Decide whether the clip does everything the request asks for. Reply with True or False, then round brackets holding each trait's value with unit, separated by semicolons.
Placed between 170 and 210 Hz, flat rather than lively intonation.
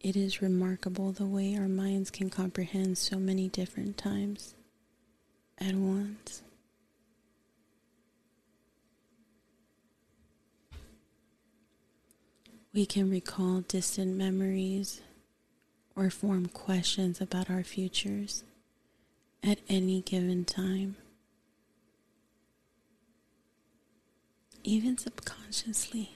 True (190 Hz; 1.3 semitones)